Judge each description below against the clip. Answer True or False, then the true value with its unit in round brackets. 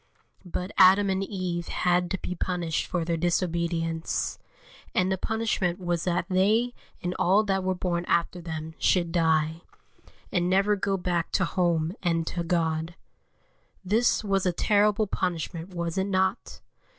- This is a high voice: False (180 Hz)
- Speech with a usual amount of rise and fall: False (2.1 semitones)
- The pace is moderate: True (150 wpm)